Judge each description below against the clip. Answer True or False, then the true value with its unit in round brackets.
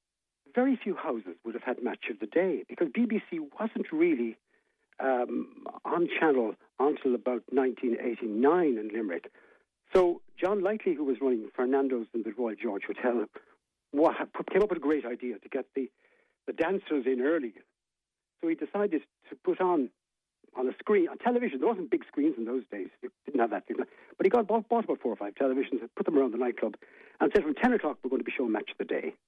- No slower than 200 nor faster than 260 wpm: True (205 wpm)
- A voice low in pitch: False (190 Hz)